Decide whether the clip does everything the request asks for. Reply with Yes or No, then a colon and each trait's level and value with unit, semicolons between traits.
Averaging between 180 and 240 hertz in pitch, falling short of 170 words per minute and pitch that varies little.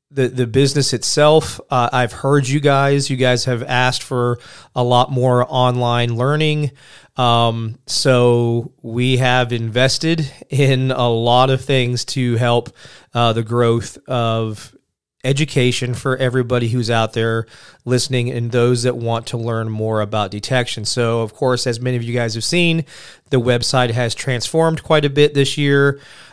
No: low, 125 Hz; average, 160 wpm; narrow, 2.1 semitones